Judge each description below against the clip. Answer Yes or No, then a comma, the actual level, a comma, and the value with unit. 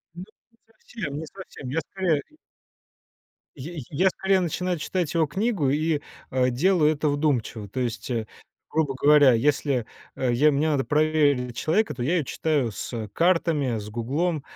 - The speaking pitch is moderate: Yes, medium, 150 Hz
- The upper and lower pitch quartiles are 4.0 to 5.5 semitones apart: Yes, average, 4.7 semitones